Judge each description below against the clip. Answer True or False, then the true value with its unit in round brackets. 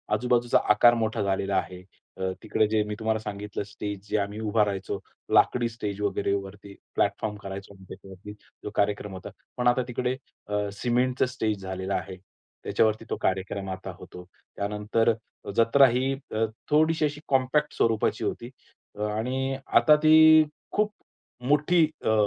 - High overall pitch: False (110 Hz)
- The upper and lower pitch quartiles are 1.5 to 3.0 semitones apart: False (3.8 semitones)